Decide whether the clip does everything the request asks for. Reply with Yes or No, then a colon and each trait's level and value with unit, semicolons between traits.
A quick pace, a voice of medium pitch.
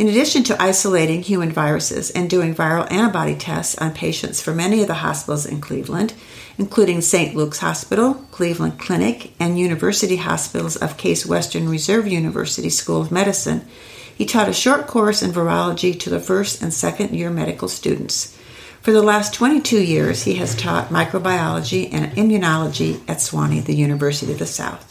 No: average, 170 wpm; medium, 175 Hz